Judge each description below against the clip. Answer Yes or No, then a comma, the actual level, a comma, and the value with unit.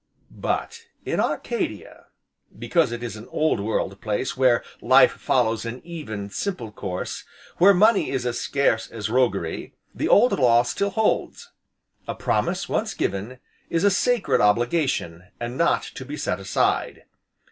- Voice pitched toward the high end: No, low, 120 Hz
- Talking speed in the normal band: Yes, average, 145 wpm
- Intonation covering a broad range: Yes, wide, 7.7 semitones